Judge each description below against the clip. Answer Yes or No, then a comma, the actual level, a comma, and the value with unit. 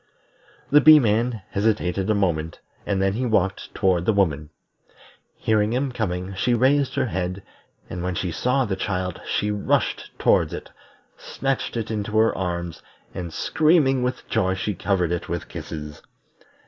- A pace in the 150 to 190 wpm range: Yes, average, 160 wpm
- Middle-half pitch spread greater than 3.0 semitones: Yes, average, 4.8 semitones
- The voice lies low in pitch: Yes, low, 100 Hz